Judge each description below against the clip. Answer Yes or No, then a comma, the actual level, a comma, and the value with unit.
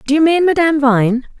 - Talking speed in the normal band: No, fast, 215 wpm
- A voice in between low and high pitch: No, very high, 285 Hz